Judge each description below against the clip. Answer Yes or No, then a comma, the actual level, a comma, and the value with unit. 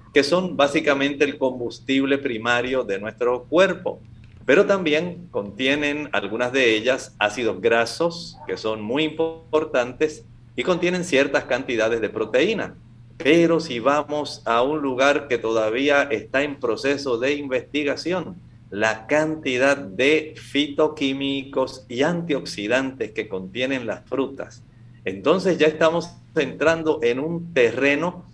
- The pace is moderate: No, slow, 120 wpm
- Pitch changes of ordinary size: Yes, average, 4.3 semitones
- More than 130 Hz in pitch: Yes, medium, 140 Hz